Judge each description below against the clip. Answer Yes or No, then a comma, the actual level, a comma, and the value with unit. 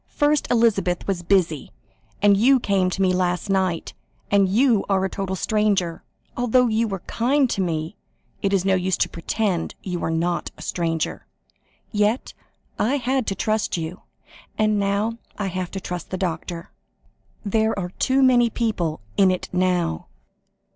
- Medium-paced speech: Yes, average, 165 wpm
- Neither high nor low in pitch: No, high, 195 Hz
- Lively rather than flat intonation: No, average, 3.6 semitones